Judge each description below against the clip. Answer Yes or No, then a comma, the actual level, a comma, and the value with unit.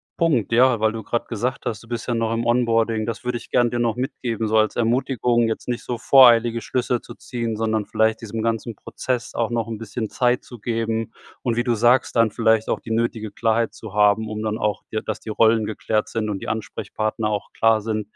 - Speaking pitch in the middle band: No, low, 115 Hz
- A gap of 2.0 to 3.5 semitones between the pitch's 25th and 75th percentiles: No, narrow, 1.5 semitones